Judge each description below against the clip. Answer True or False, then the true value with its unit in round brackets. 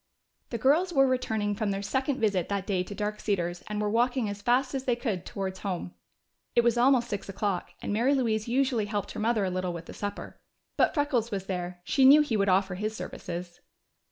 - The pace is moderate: False (215 wpm)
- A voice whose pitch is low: False (210 Hz)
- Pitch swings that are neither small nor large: True (4.1 semitones)